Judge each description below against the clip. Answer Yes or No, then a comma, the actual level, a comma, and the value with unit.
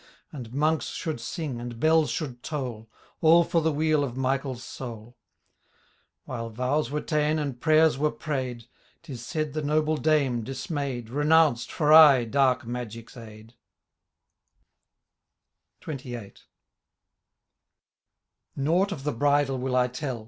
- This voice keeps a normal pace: No, slow, 125 wpm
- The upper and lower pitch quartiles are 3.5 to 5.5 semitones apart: Yes, average, 4.0 semitones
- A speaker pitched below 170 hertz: Yes, low, 135 Hz